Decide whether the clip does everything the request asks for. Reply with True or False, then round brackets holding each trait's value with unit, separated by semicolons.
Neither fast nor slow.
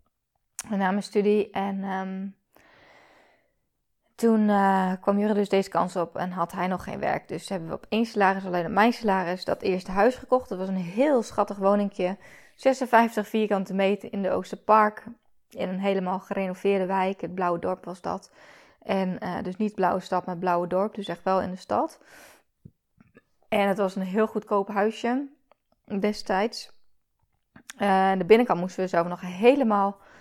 True (175 wpm)